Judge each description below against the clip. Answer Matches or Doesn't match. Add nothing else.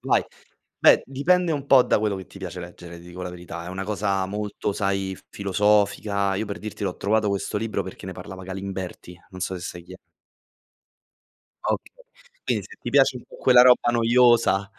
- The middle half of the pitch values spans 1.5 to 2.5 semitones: Doesn't match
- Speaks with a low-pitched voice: Matches